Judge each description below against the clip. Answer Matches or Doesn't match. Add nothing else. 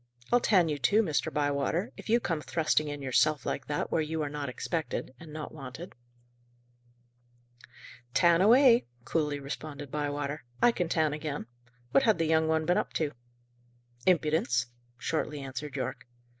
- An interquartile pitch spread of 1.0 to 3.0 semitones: Matches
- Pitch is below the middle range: Doesn't match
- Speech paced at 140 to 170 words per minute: Matches